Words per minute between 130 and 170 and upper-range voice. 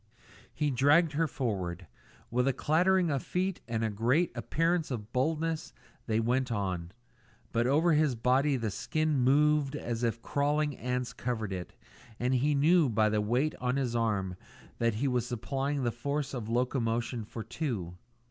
No: average, 165 wpm; low, 125 Hz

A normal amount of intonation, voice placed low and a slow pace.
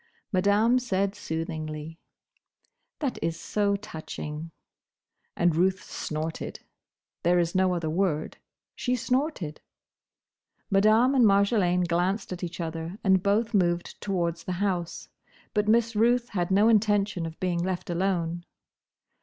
No: average, 3.5 semitones; medium, 185 Hz; slow, 125 wpm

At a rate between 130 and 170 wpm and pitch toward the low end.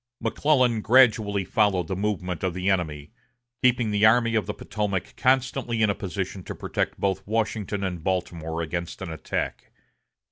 Yes: average, 155 wpm; low, 100 Hz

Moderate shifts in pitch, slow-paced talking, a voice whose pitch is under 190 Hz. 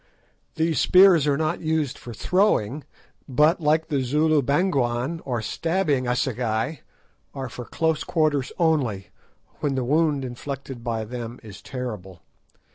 Yes: average, 4.6 semitones; slow, 130 wpm; medium, 140 Hz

